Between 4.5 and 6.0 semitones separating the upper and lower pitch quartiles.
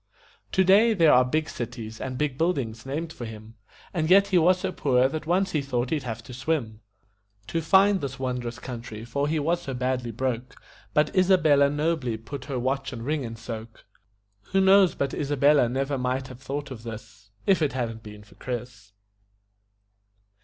Yes: average, 4.8 semitones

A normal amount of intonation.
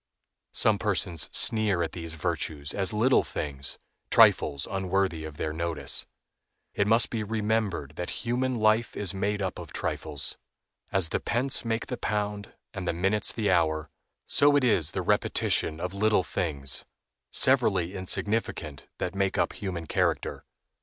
Yes: average, 4.7 semitones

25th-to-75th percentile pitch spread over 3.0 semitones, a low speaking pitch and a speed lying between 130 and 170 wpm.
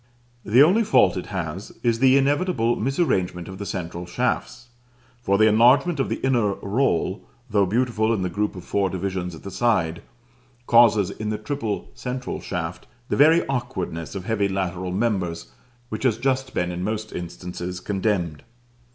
Yes: average, 5.1 semitones; low, 105 Hz; average, 165 wpm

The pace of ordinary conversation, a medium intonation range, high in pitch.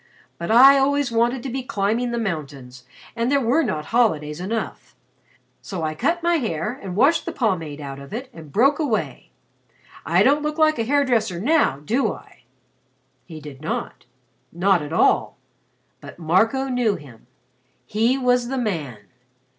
No: average, 165 wpm; wide, 8.5 semitones; high, 225 Hz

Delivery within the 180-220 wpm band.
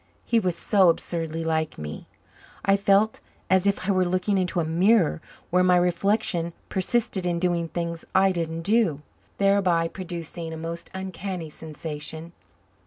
No: average, 150 wpm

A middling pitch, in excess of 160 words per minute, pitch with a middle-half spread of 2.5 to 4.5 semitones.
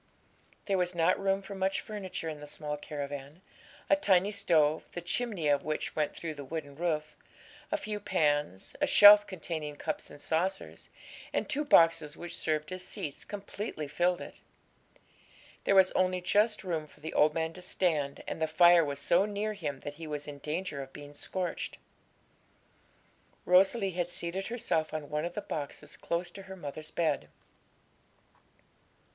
Yes: medium, 170 Hz; average, 170 wpm; average, 4.1 semitones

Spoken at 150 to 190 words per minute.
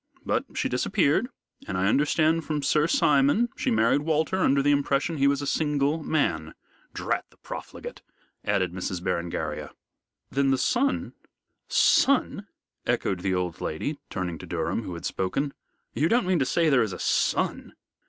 Yes: average, 165 wpm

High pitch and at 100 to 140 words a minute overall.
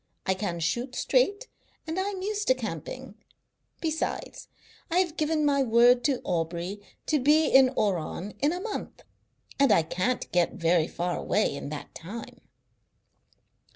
No: high, 245 Hz; average, 155 wpm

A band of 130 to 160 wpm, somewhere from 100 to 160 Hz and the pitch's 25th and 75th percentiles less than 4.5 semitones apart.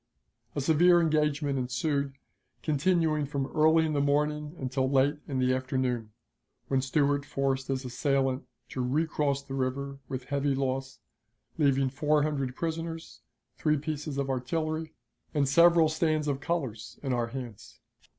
Yes: average, 140 wpm; medium, 140 Hz; narrow, 2.6 semitones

